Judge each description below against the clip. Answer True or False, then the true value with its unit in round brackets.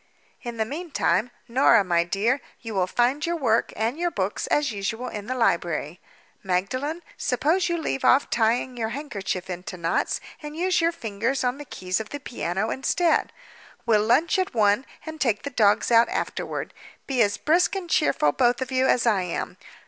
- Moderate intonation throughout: False (6.1 semitones)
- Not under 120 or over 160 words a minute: False (185 wpm)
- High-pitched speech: True (240 Hz)